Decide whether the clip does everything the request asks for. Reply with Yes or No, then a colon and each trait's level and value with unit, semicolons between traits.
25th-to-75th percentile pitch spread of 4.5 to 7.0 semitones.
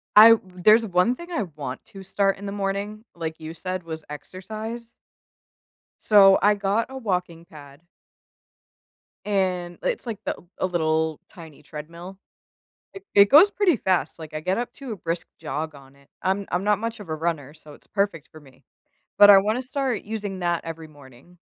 Yes: average, 4.9 semitones